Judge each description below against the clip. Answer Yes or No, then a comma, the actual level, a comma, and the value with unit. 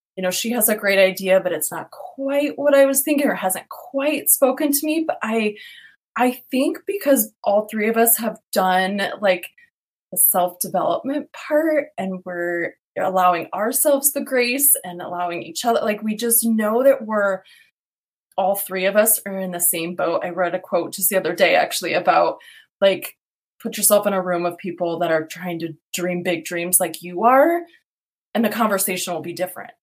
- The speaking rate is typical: Yes, average, 190 wpm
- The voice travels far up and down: Yes, wide, 6.6 semitones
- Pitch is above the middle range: Yes, high, 205 Hz